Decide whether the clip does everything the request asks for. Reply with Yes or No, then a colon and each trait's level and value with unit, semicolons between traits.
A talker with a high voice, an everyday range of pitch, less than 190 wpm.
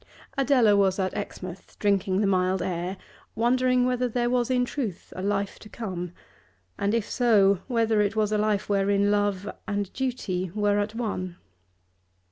Yes: high, 205 Hz; average, 3.3 semitones; average, 160 wpm